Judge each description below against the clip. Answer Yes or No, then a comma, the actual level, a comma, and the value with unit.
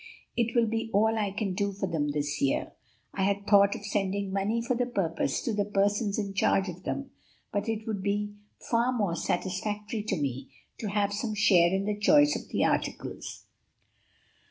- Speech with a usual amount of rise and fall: No, narrow, 2.3 semitones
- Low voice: No, high, 205 Hz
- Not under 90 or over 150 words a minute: No, average, 190 wpm